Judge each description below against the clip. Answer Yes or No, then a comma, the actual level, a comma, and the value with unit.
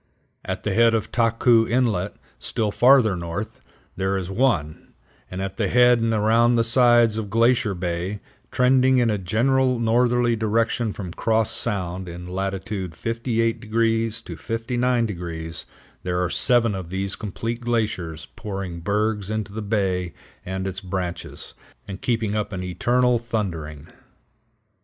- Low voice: Yes, low, 110 Hz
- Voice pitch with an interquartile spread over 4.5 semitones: No, average, 3.8 semitones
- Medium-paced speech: Yes, average, 145 wpm